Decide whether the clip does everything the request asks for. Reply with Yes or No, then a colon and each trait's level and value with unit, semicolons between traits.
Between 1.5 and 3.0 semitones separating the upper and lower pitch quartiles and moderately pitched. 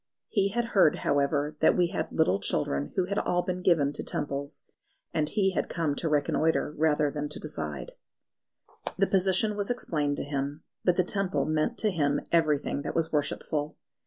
No: average, 4.3 semitones; medium, 155 Hz